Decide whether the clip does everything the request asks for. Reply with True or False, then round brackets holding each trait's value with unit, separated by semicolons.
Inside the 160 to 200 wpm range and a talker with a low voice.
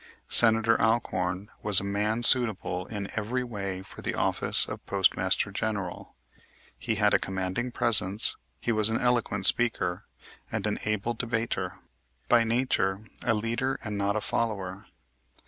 False (145 wpm; 105 Hz)